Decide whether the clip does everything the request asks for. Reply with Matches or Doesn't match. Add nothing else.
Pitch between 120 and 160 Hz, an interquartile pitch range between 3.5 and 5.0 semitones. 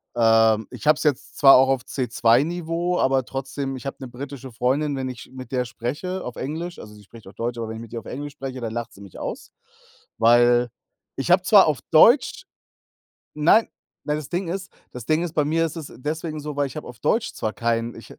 Matches